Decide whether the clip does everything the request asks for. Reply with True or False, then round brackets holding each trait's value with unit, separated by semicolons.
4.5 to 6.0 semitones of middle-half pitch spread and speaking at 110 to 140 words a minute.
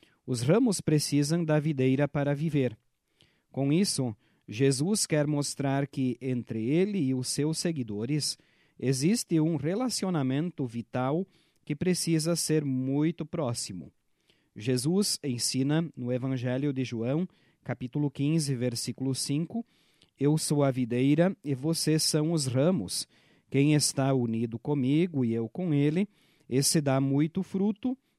False (3.9 semitones; 125 wpm)